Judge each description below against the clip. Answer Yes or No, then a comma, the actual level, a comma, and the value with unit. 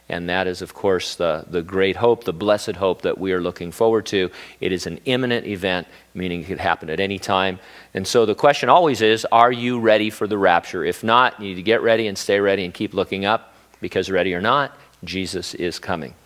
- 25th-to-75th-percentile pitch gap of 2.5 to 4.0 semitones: Yes, average, 3.5 semitones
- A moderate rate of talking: No, fast, 235 wpm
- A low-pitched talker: Yes, low, 100 Hz